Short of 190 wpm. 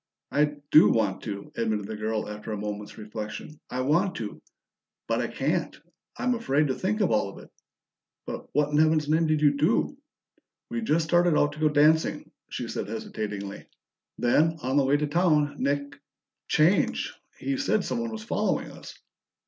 Yes: average, 175 wpm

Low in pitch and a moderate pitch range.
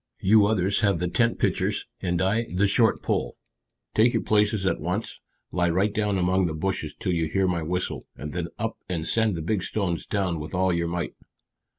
Yes: very low, 95 Hz; average, 3.2 semitones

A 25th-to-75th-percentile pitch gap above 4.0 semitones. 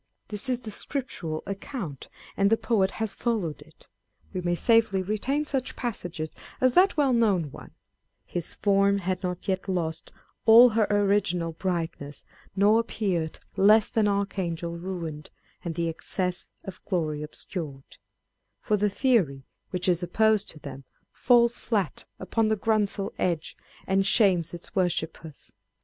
Yes: average, 4.4 semitones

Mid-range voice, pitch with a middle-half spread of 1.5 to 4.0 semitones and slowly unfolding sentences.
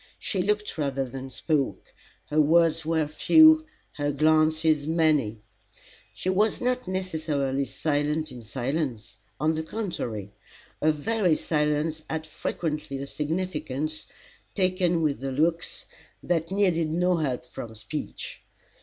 Yes: medium, 155 Hz; average, 3.4 semitones; slow, 125 wpm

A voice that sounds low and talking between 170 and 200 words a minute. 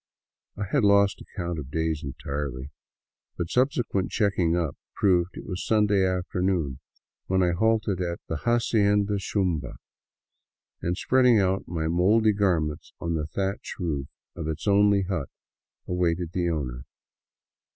No: very low, 90 Hz; average, 145 wpm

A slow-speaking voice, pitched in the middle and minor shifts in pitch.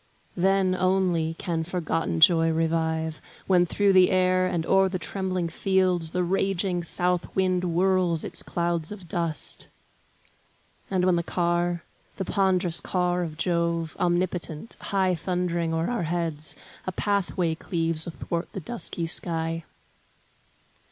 Yes: slow, 130 wpm; medium, 175 Hz; narrow, 2.0 semitones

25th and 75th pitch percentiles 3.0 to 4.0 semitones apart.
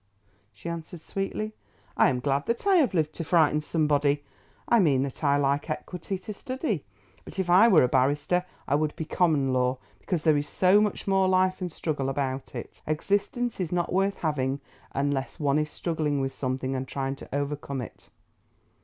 No: average, 5.0 semitones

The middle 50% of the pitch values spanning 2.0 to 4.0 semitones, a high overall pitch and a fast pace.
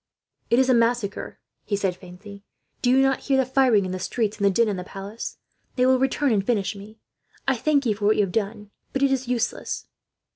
No: average, 4.4 semitones; high, 225 Hz; fast, 230 wpm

